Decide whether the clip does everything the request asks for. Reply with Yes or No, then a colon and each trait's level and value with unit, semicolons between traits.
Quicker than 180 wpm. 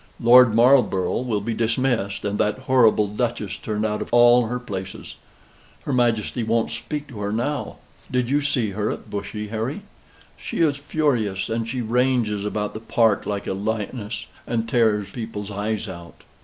No: average, 170 wpm